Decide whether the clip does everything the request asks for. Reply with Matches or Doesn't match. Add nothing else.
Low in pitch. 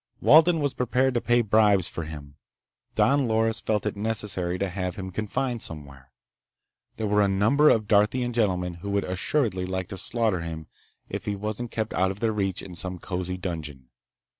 Matches